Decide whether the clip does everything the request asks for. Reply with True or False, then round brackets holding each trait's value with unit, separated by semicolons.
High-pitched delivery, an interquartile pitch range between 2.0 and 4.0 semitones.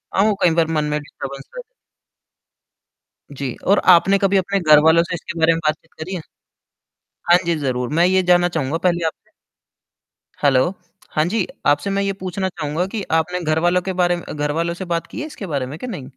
False (170 Hz; 3.6 semitones)